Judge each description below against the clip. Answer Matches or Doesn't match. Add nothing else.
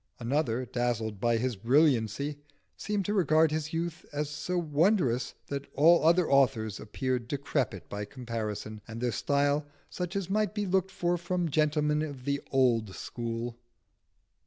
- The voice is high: Doesn't match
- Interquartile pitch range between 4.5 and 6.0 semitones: Matches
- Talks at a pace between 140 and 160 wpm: Matches